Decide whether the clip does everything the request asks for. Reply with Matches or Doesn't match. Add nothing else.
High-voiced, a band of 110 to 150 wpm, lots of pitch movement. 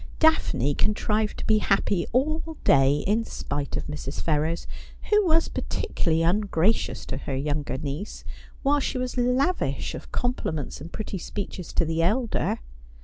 Matches